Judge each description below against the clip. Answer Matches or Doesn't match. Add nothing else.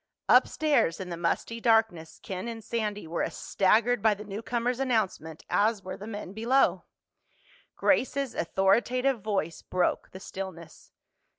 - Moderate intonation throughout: Matches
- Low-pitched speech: Doesn't match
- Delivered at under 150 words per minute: Matches